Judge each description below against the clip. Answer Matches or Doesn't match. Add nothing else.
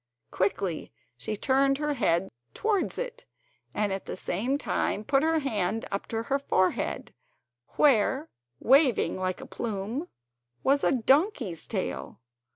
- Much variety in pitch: Matches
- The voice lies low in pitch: Doesn't match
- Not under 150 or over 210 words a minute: Doesn't match